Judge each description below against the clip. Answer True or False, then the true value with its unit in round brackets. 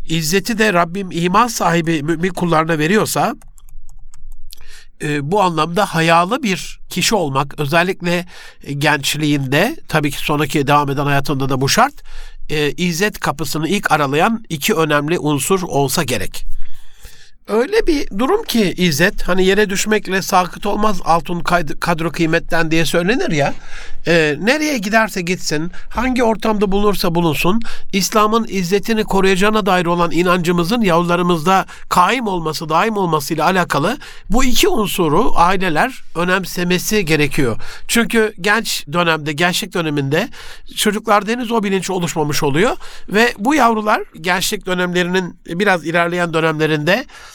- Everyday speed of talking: True (120 wpm)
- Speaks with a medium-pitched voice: True (180 Hz)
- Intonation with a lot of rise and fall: False (4.5 semitones)